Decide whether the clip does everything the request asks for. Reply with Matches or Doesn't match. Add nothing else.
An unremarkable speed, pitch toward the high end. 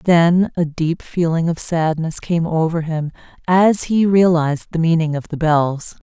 Doesn't match